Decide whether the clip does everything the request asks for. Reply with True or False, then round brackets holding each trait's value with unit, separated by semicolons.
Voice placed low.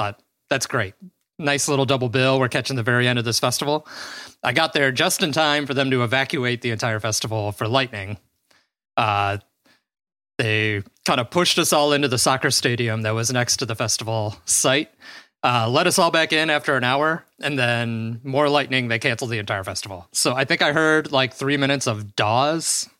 True (130 Hz)